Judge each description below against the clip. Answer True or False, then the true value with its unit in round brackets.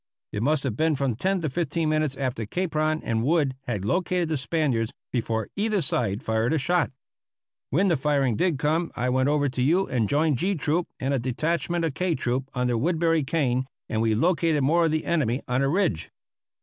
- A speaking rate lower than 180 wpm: False (200 wpm)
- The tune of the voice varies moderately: True (4.9 semitones)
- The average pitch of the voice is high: False (145 Hz)